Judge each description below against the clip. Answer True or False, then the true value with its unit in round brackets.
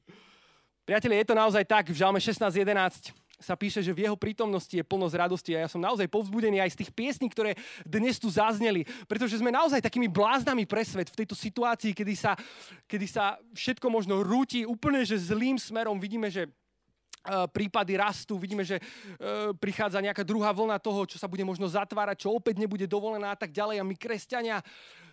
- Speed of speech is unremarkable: False (185 wpm)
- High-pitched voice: True (210 Hz)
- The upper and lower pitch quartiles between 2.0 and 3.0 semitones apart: True (2.4 semitones)